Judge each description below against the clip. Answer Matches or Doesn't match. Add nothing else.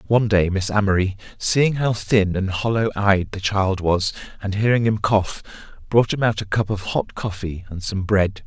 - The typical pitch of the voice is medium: Doesn't match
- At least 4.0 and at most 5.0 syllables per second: Matches